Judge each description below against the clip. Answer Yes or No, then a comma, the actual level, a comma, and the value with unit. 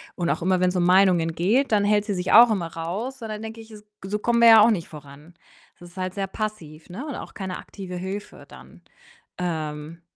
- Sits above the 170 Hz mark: Yes, high, 190 Hz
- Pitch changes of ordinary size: Yes, average, 3.7 semitones